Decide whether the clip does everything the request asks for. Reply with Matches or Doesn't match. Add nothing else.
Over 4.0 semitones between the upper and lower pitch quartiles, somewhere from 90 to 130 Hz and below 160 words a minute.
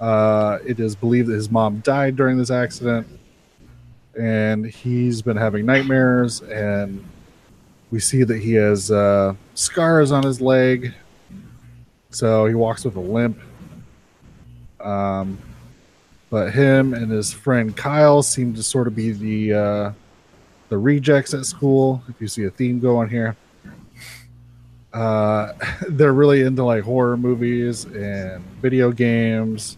Doesn't match